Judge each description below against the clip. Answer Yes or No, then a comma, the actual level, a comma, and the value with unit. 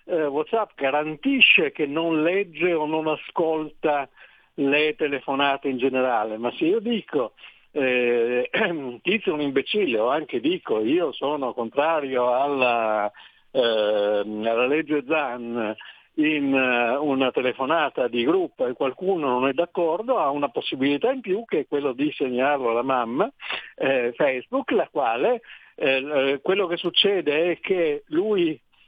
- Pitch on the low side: No, medium, 150 Hz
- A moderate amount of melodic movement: No, wide, 6.0 semitones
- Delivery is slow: No, average, 140 wpm